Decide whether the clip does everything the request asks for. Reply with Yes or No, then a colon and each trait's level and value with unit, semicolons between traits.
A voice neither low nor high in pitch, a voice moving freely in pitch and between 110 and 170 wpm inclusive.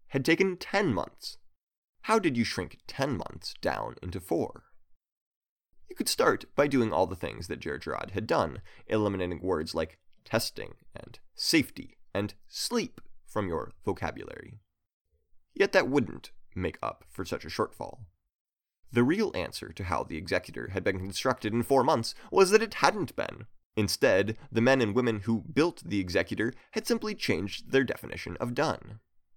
No: low, 115 Hz; wide, 6.2 semitones; average, 160 wpm